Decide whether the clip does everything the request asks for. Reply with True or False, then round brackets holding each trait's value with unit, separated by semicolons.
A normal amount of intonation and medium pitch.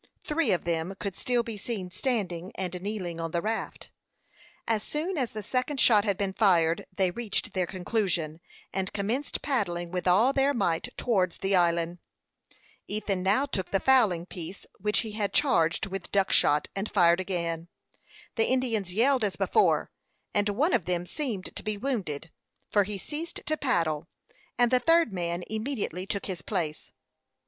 False (4.8 semitones; 200 Hz)